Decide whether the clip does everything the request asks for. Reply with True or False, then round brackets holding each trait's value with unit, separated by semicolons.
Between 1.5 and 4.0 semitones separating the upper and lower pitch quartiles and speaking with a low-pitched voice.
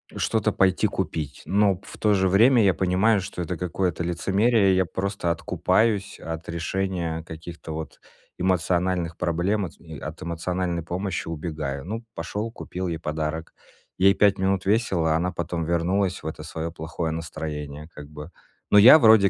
True (3.2 semitones; 90 Hz)